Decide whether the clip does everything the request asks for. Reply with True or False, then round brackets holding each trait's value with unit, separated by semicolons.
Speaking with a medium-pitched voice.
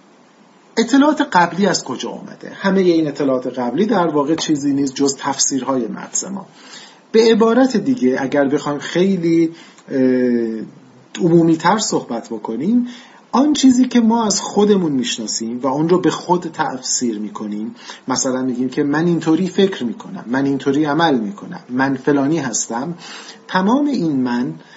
True (165 Hz)